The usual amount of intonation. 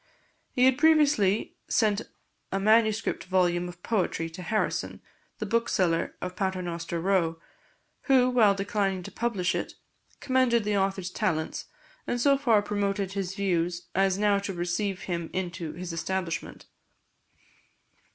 Yes: average, 3.4 semitones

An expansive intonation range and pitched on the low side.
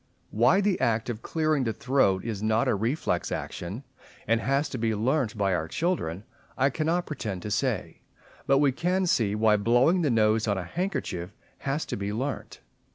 Yes: wide, 5.7 semitones; low, 115 Hz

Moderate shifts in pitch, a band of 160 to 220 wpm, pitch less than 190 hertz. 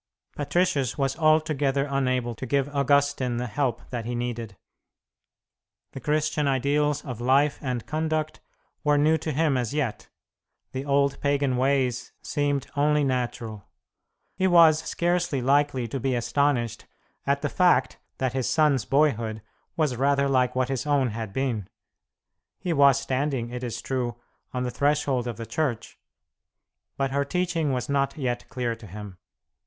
No: average, 3.0 semitones; average, 150 wpm; low, 135 Hz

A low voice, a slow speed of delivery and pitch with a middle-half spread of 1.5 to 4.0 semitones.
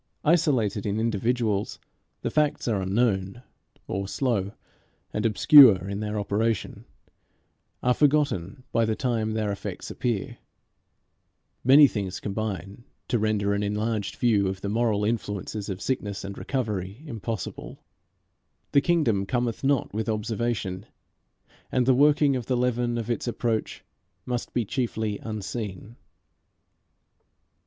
Yes: low, 110 Hz; slow, 125 wpm; average, 3.3 semitones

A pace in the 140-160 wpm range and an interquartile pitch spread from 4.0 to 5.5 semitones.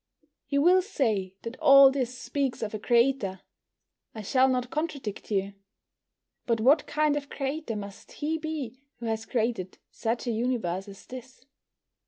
Yes: average, 155 wpm; average, 4.3 semitones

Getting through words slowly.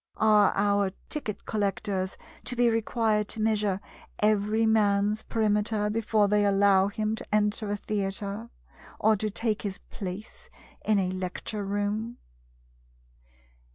Yes: slow, 125 wpm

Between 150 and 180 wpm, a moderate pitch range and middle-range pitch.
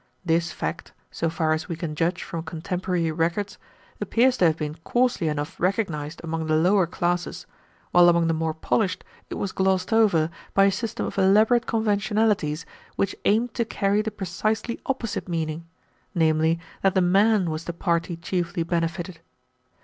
Yes: average, 165 wpm; average, 3.7 semitones; medium, 175 Hz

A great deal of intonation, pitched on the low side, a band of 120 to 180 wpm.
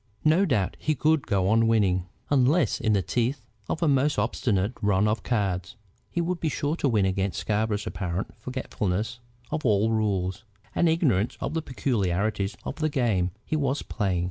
Yes: wide, 6.3 semitones; low, 110 Hz; average, 175 wpm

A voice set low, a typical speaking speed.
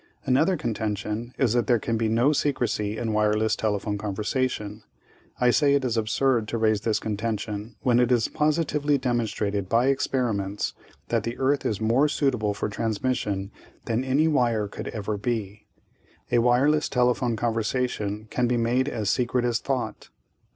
Yes: low, 115 Hz; average, 160 wpm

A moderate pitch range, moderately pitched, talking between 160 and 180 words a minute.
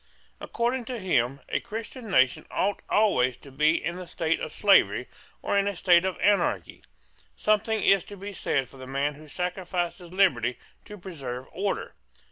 No: wide, 6.5 semitones; medium, 180 Hz; average, 170 wpm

